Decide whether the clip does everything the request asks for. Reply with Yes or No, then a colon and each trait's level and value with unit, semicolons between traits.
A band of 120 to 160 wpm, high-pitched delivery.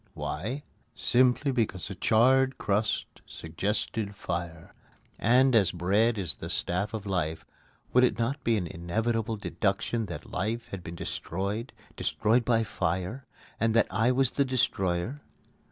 No: average, 140 wpm; low, 110 Hz